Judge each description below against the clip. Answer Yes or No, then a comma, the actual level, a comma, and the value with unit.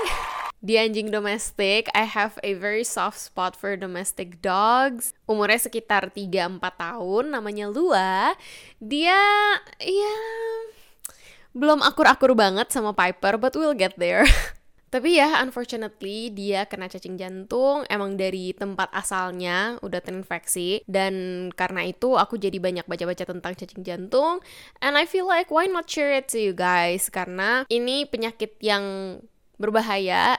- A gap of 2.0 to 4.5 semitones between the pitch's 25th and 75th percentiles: No, average, 5.2 semitones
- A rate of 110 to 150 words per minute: Yes, average, 135 wpm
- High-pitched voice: Yes, high, 210 Hz